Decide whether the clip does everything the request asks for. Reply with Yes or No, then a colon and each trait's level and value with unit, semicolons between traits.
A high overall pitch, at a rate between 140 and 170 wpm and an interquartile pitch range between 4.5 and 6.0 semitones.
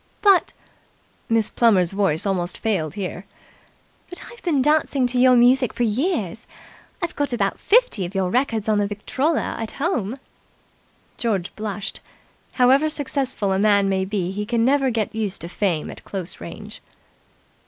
Yes: high, 220 Hz; average, 160 wpm; average, 5.3 semitones